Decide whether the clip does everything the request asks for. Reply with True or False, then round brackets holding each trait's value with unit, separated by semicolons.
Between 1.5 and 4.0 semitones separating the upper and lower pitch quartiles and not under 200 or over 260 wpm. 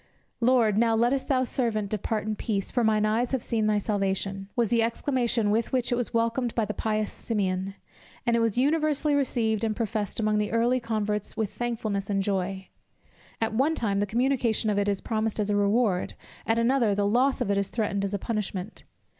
True (2.7 semitones; 205 wpm)